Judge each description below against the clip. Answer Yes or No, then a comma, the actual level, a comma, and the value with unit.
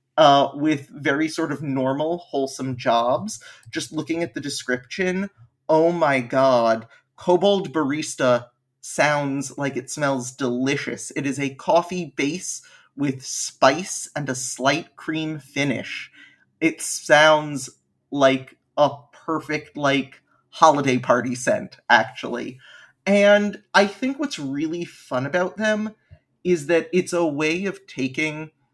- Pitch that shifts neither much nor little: Yes, average, 3.8 semitones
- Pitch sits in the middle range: Yes, medium, 145 Hz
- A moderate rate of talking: No, slow, 125 wpm